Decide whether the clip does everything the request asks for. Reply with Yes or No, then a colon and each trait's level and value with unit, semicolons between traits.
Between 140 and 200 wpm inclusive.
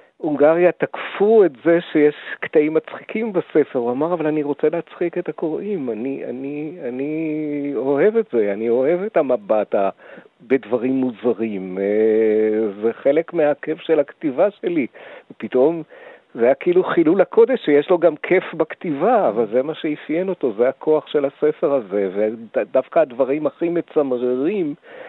Yes: average, 145 wpm